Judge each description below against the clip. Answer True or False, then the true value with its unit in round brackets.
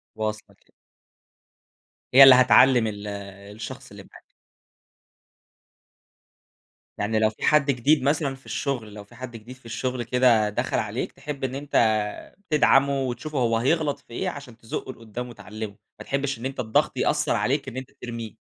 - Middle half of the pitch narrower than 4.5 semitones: True (3.5 semitones)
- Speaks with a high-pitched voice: False (125 Hz)